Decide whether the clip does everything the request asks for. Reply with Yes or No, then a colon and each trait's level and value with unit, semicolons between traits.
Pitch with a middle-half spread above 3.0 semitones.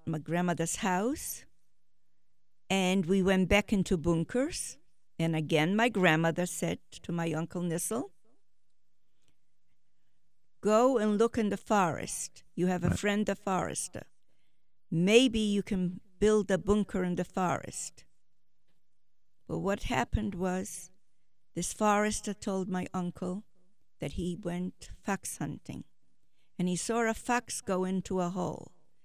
No: average, 2.7 semitones